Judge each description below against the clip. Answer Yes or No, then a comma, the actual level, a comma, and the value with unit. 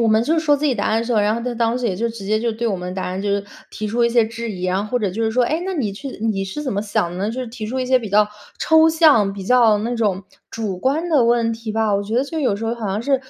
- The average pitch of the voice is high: Yes, high, 225 Hz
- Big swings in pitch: No, average, 3.4 semitones